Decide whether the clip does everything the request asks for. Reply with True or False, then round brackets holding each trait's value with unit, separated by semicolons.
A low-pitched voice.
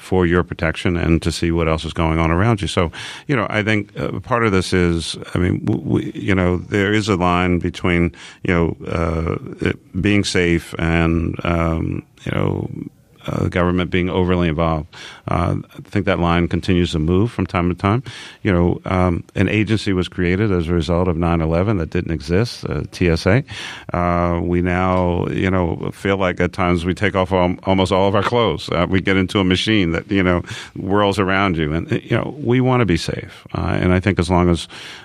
True (90 Hz)